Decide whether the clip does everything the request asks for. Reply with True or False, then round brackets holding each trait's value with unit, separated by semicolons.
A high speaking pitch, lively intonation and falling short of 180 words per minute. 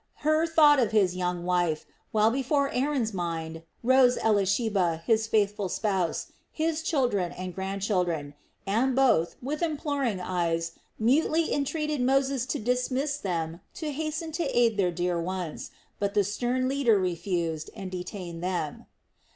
True (210 Hz; 7.1 semitones; 140 wpm)